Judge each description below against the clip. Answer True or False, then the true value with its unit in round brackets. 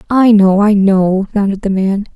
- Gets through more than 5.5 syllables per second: False (4.4 syllables/s)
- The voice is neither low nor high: False (200 Hz)